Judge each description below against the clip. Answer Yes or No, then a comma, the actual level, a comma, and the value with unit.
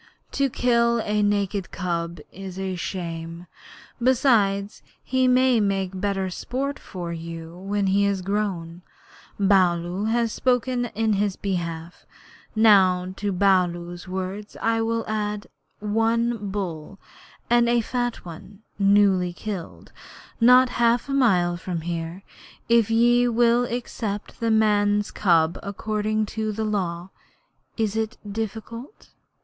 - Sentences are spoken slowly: Yes, slow, 120 wpm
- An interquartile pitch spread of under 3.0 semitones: No, average, 3.8 semitones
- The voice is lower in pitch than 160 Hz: No, high, 205 Hz